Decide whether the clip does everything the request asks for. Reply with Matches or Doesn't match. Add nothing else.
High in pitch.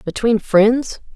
Matches